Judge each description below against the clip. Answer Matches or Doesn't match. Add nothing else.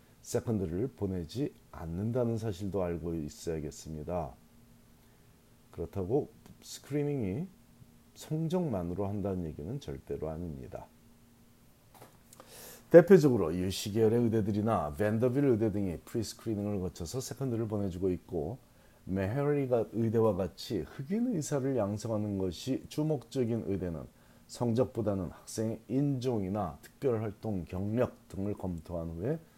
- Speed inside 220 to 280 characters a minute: Doesn't match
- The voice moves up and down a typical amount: Matches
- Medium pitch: Doesn't match